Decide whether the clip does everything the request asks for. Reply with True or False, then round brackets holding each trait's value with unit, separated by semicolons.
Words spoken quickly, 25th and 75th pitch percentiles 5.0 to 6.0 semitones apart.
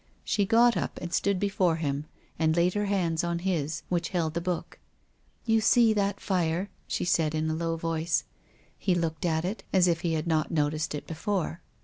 False (215 wpm; 3.1 semitones)